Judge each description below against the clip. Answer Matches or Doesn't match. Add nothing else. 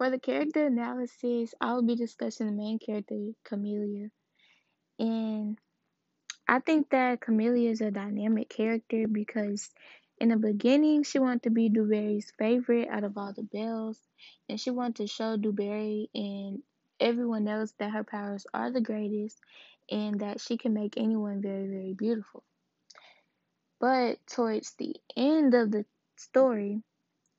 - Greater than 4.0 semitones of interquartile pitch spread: Doesn't match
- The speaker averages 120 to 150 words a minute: Matches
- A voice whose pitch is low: Doesn't match